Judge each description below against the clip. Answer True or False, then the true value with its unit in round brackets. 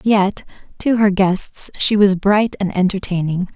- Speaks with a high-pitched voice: True (195 Hz)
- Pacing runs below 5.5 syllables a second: True (4.0 syllables/s)